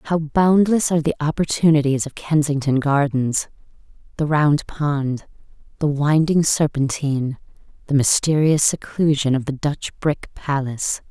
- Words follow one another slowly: Yes, slow, 115 wpm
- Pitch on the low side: No, medium, 150 Hz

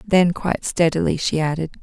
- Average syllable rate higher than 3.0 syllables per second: Yes, 5.5 syllables/s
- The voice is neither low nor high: Yes, medium, 165 Hz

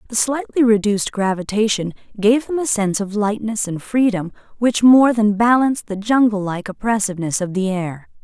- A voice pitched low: No, high, 215 Hz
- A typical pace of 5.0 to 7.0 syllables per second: Yes, 5.4 syllables/s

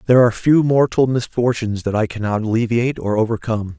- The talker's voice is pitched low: Yes, low, 115 Hz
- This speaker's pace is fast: No, average, 175 wpm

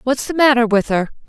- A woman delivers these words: Yes, female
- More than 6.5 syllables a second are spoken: No, 5.9 syllables/s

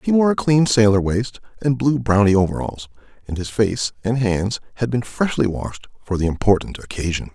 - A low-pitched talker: Yes, low, 110 Hz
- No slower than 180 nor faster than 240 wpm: Yes, average, 190 wpm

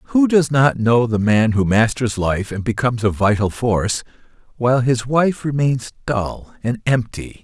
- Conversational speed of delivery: Yes, average, 170 wpm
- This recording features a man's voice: Yes, male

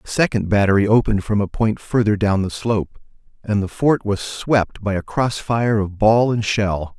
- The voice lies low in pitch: Yes, low, 105 Hz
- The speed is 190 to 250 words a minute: Yes, fast, 205 wpm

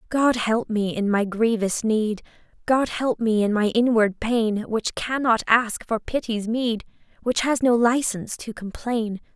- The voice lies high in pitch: Yes, high, 225 Hz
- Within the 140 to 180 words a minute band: Yes, average, 165 wpm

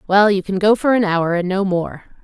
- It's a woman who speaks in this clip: Yes, female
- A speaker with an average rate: No, fast, 270 wpm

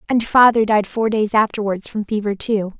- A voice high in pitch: Yes, high, 215 Hz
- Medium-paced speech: Yes, average, 195 wpm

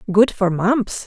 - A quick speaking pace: No, average, 170 wpm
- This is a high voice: Yes, high, 205 Hz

